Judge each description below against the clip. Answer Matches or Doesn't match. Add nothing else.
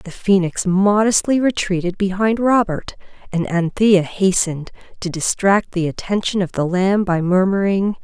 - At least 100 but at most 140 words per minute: Matches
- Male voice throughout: Doesn't match